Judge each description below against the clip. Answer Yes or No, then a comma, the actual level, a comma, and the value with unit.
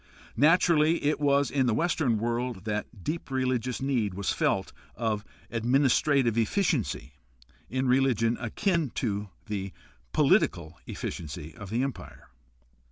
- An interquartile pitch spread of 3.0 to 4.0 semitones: No, average, 4.6 semitones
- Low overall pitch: Yes, low, 125 Hz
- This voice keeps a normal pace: No, slow, 125 wpm